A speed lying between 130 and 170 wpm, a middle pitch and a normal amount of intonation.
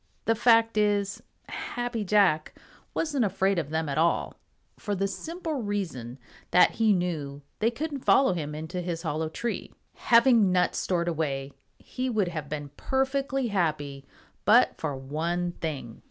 No: average, 150 wpm; medium, 180 Hz; wide, 6.6 semitones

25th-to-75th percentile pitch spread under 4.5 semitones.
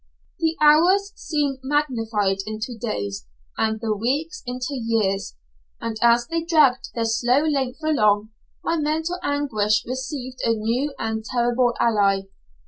No: average, 5.0 semitones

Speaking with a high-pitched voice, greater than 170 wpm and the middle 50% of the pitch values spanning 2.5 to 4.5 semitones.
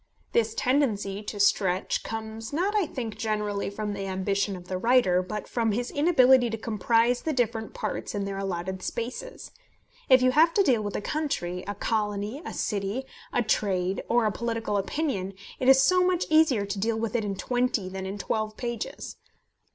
Yes: high, 220 Hz; average, 185 wpm; average, 4.0 semitones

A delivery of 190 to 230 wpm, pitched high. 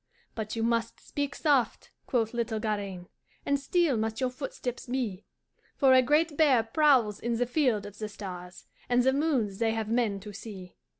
No: average, 180 wpm; high, 235 Hz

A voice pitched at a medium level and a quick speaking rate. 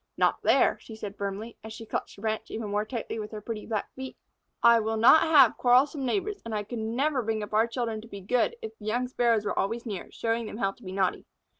No: high, 225 Hz; fast, 250 wpm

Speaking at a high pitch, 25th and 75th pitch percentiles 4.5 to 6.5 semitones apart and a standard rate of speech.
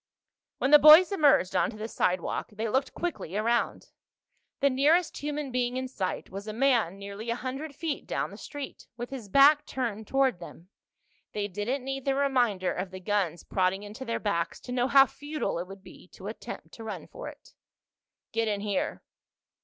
Yes: high, 235 Hz; average, 5.3 semitones; average, 185 wpm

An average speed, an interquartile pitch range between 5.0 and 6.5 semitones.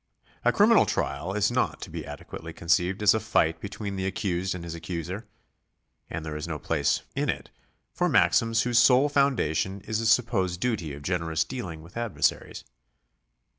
Yes: average, 170 wpm; wide, 5.4 semitones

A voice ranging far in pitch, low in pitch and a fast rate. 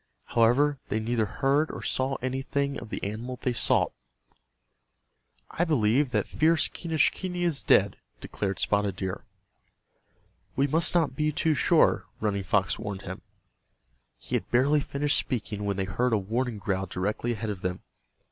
No: wide, 5.9 semitones; low, 120 Hz; average, 155 wpm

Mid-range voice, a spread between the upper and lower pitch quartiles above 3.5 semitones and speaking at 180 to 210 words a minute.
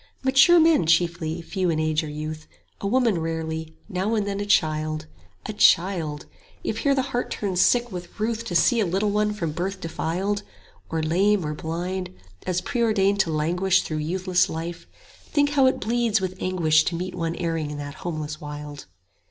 Yes: medium, 180 Hz; average, 4.5 semitones; average, 185 wpm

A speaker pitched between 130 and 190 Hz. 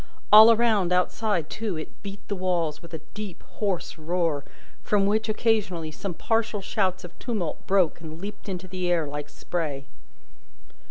Yes: medium, 185 Hz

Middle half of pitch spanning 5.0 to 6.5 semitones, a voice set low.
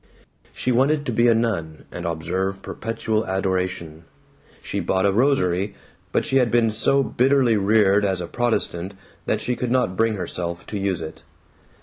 No: average, 4.5 semitones; low, 100 Hz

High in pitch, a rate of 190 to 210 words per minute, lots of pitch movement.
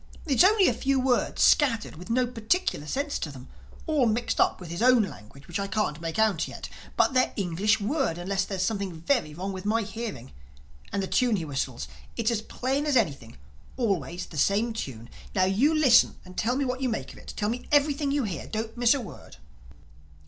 Yes: high, 215 Hz; average, 200 wpm; wide, 6.8 semitones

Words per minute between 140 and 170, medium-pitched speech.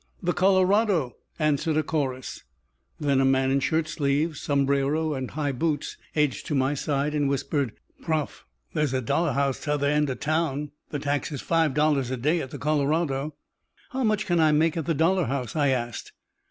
No: average, 180 wpm; medium, 150 Hz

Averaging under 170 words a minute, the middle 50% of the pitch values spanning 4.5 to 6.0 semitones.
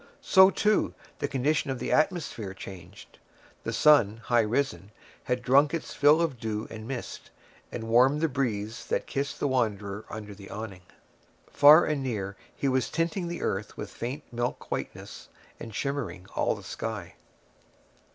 Yes: average, 160 wpm; average, 5.1 semitones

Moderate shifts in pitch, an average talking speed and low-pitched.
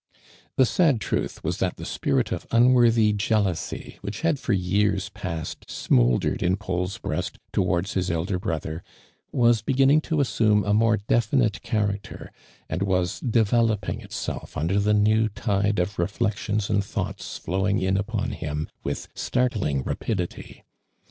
Yes: average, 3.5 semitones; average, 150 wpm; low, 105 Hz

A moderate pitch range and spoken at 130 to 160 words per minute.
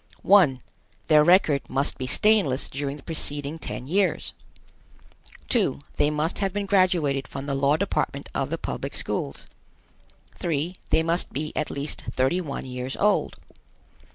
Yes: average, 4.6 semitones; average, 150 wpm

